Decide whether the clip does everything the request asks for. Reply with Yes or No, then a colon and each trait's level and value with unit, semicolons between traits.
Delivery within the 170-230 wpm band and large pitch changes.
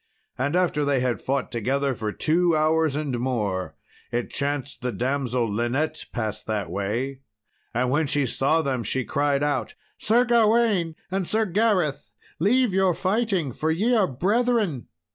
No: average, 155 wpm; wide, 6.6 semitones